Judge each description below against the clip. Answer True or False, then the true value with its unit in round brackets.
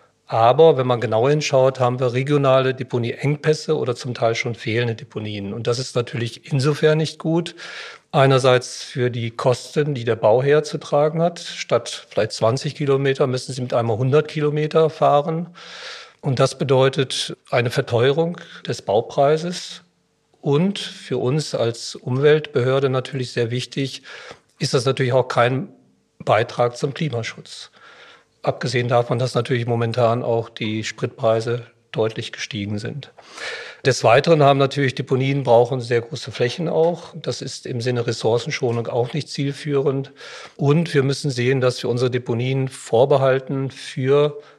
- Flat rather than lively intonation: False (3.4 semitones)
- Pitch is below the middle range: True (130 Hz)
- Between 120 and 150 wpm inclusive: True (140 wpm)